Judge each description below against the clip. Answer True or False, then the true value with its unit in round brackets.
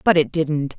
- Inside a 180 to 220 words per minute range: False (230 wpm)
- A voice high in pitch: False (155 Hz)